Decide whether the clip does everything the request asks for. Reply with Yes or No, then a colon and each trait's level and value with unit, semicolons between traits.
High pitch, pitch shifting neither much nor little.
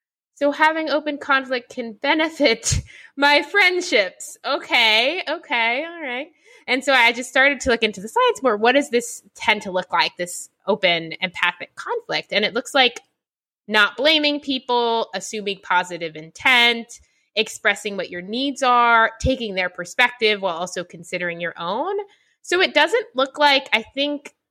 No: high, 245 Hz; wide, 5.8 semitones